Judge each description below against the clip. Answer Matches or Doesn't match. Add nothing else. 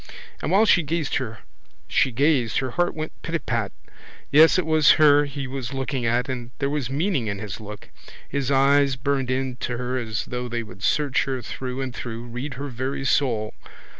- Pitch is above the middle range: Doesn't match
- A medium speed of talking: Matches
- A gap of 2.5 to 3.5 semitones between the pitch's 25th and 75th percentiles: Matches